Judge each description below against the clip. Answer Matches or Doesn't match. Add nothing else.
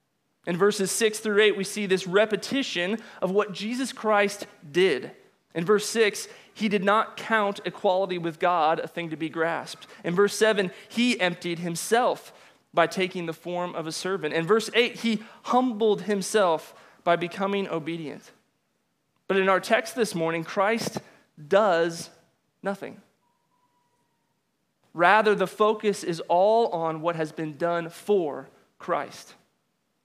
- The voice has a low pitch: Doesn't match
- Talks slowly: Doesn't match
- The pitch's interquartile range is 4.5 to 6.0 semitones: Doesn't match